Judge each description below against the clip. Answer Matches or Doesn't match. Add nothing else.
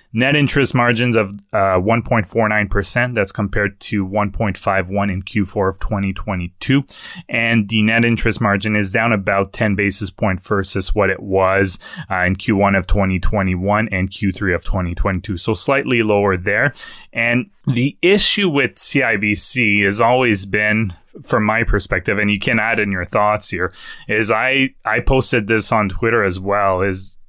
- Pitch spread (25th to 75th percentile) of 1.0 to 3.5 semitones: Matches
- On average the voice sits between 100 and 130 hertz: Matches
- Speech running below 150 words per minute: Doesn't match